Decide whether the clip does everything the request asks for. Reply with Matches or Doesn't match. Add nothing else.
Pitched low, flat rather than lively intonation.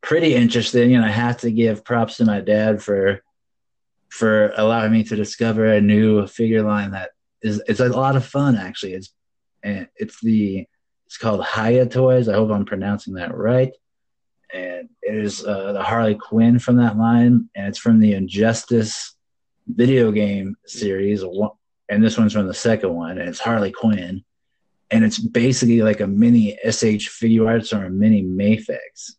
Matches